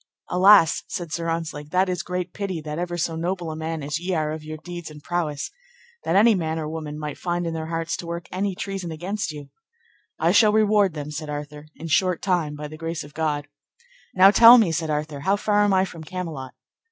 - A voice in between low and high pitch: Yes, medium, 165 Hz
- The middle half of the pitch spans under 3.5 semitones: Yes, average, 3.1 semitones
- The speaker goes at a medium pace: No, fast, 225 wpm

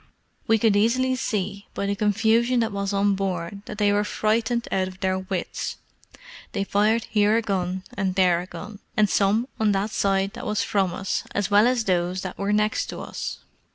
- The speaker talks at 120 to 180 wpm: No, average, 200 wpm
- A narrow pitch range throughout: Yes, narrow, 2.2 semitones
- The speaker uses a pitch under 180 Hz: No, high, 205 Hz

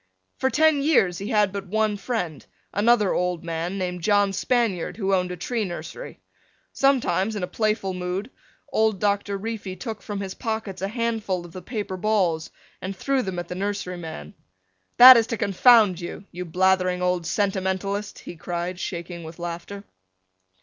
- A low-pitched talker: No, high, 195 Hz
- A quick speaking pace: No, average, 170 wpm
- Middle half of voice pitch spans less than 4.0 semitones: Yes, average, 3.3 semitones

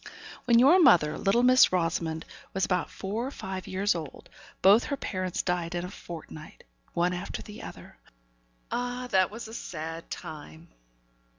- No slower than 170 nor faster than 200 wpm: No, average, 160 wpm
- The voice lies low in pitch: No, medium, 185 Hz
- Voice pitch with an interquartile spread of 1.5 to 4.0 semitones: No, average, 5.0 semitones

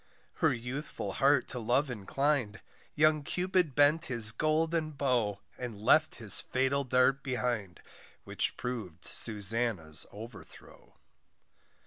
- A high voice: No, low, 125 Hz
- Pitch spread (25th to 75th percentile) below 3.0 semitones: No, average, 4.9 semitones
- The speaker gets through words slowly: Yes, slow, 110 wpm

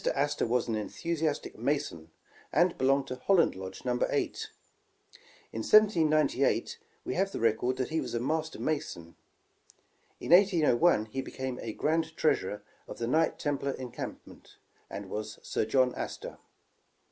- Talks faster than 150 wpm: No, average, 140 wpm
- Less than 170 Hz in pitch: Yes, low, 135 Hz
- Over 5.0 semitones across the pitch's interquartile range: Yes, wide, 5.5 semitones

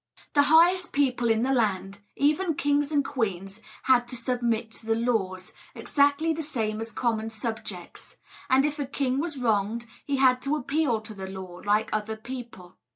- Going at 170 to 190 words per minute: Yes, average, 175 wpm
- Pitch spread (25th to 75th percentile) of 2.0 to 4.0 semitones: No, average, 4.7 semitones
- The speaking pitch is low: No, high, 240 Hz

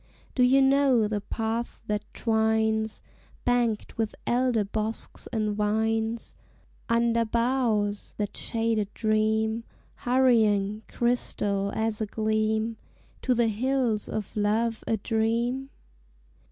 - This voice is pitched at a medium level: No, high, 220 Hz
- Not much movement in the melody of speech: Yes, narrow, 1.6 semitones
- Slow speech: Yes, slow, 115 wpm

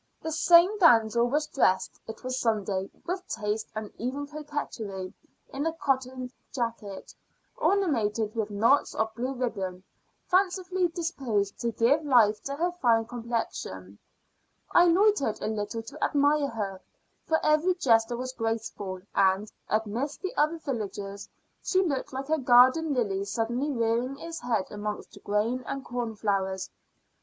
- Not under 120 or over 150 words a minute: Yes, average, 140 wpm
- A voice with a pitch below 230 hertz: No, high, 240 Hz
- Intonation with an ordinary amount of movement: No, wide, 5.7 semitones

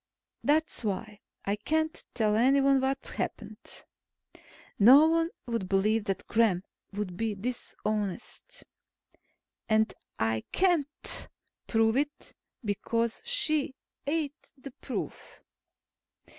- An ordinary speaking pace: No, slow, 100 wpm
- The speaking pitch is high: Yes, high, 230 Hz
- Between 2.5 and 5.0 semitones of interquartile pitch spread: No, wide, 5.6 semitones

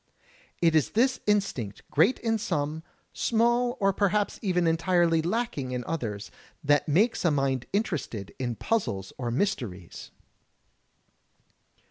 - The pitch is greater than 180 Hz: No, medium, 165 Hz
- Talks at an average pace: No, slow, 120 wpm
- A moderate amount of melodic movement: No, wide, 8.2 semitones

